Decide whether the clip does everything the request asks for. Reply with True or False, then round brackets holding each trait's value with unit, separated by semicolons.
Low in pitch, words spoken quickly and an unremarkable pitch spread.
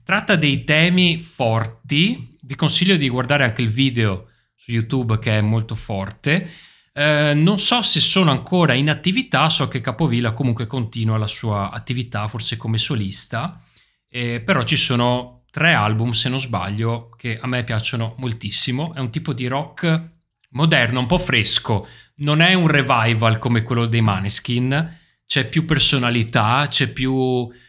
False (130 Hz; 155 wpm; 5.0 semitones)